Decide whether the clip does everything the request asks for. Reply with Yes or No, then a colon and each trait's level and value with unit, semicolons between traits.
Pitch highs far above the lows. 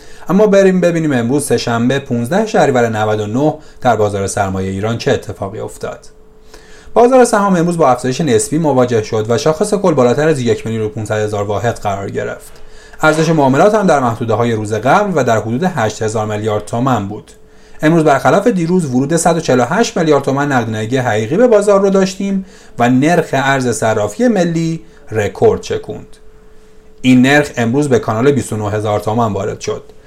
Yes: wide, 7.0 semitones